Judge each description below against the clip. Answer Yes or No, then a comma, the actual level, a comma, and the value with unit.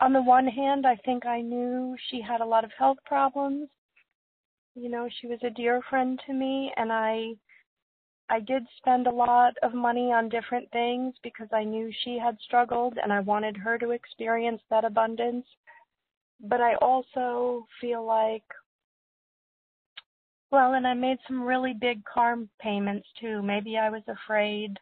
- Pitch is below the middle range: No, high, 240 Hz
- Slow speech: No, average, 165 wpm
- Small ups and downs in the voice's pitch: Yes, narrow, 2.1 semitones